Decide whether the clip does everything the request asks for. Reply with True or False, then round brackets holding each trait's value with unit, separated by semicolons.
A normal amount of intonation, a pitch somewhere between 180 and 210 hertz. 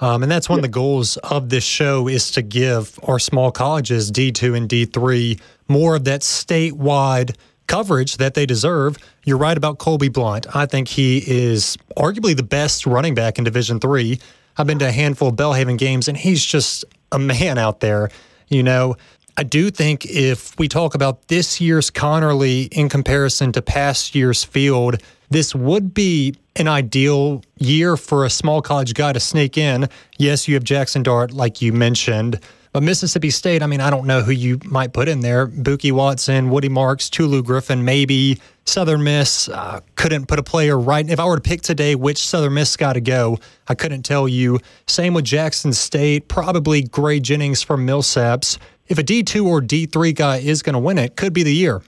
False (3.0 semitones; 140 Hz)